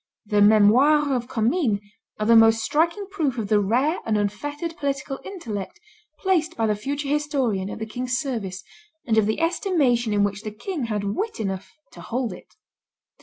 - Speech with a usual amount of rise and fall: No, wide, 5.8 semitones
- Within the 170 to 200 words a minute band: Yes, average, 175 wpm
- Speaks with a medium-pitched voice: No, high, 240 Hz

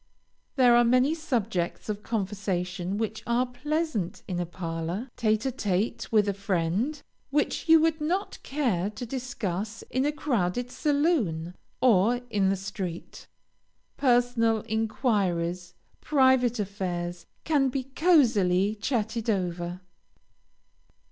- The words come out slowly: Yes, slow, 120 wpm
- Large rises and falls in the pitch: Yes, wide, 5.7 semitones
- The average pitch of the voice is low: No, high, 220 Hz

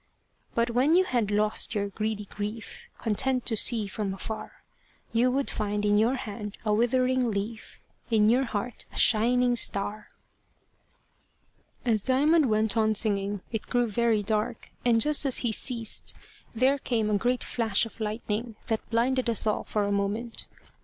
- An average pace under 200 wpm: Yes, average, 160 wpm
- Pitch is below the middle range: No, high, 225 Hz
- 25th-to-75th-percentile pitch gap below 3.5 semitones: Yes, narrow, 2.6 semitones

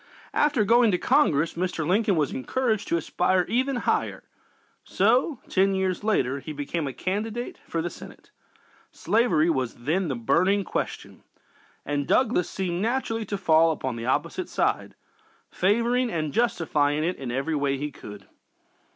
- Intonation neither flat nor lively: No, wide, 7.0 semitones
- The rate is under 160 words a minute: Yes, average, 150 wpm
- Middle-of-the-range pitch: Yes, medium, 180 Hz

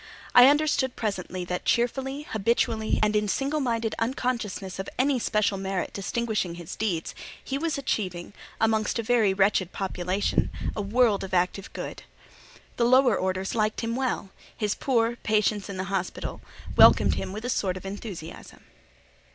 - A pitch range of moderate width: Yes, average, 3.9 semitones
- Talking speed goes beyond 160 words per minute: No, average, 150 wpm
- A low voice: No, high, 215 Hz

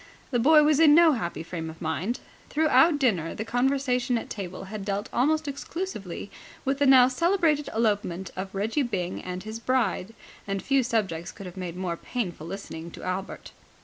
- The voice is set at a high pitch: Yes, high, 220 Hz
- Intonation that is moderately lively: No, wide, 6.8 semitones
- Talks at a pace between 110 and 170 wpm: No, average, 180 wpm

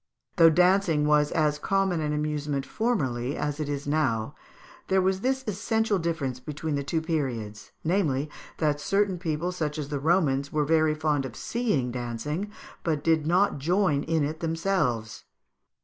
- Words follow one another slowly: No, average, 160 wpm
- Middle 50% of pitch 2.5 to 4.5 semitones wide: Yes, average, 3.9 semitones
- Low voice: No, medium, 155 Hz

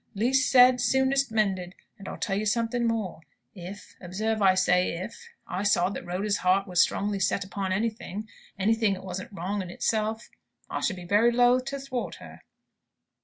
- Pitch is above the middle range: Yes, high, 205 Hz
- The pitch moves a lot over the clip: No, average, 3.6 semitones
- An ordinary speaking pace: Yes, average, 175 wpm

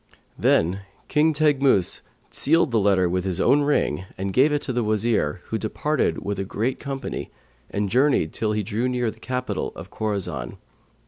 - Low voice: Yes, low, 110 Hz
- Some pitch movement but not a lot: No, wide, 5.8 semitones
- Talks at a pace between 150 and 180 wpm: Yes, average, 175 wpm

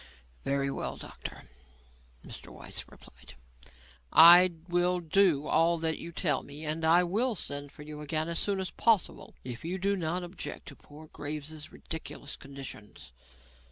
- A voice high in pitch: No, medium, 160 Hz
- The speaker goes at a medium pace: Yes, average, 155 wpm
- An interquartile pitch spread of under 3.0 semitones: No, average, 3.5 semitones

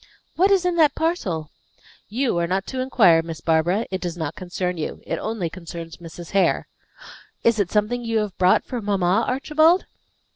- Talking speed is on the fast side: No, average, 180 wpm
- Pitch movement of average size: No, wide, 6.5 semitones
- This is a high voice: Yes, high, 195 Hz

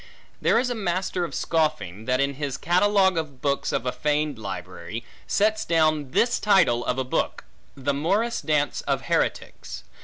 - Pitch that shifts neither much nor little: No, wide, 6.6 semitones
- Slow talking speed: No, average, 165 wpm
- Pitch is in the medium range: Yes, medium, 150 Hz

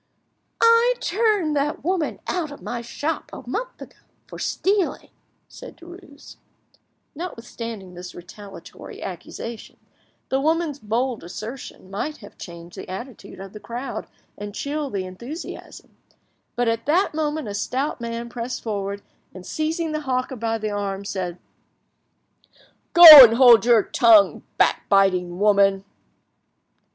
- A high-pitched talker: Yes, high, 235 Hz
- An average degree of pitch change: No, wide, 7.2 semitones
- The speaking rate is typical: No, slow, 130 wpm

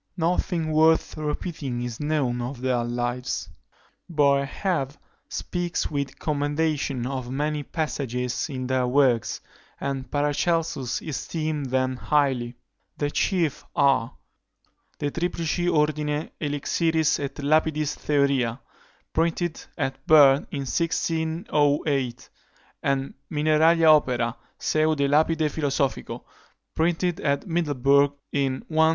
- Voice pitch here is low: No, medium, 145 Hz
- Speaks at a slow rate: Yes, slow, 105 wpm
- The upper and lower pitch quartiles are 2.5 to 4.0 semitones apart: Yes, average, 2.9 semitones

